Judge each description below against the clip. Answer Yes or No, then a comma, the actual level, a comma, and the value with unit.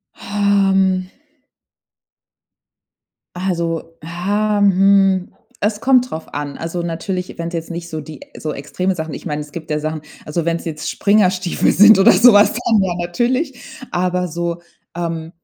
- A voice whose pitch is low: No, medium, 180 Hz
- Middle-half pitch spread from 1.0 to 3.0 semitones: No, average, 3.4 semitones